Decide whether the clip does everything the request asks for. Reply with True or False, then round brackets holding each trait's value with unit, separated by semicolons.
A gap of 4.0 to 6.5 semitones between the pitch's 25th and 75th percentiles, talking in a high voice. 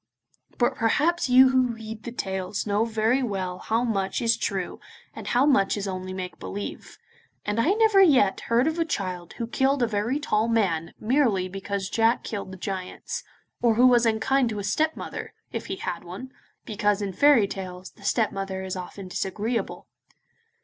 True (4.4 semitones; 220 Hz)